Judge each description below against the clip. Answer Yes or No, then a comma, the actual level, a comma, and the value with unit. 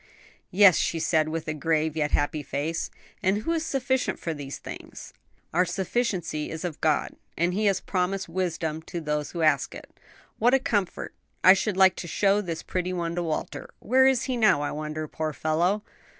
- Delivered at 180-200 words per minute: Yes, average, 190 wpm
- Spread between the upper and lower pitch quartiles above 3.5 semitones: Yes, average, 4.2 semitones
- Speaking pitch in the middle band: Yes, medium, 175 Hz